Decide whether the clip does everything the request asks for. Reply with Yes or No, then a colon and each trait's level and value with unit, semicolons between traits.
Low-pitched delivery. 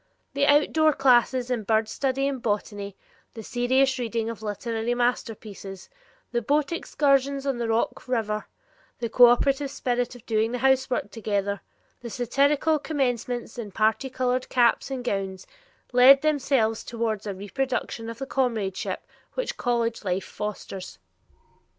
No: high, 240 Hz